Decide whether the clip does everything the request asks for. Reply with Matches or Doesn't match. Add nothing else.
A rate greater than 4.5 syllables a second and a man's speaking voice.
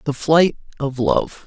Doesn't match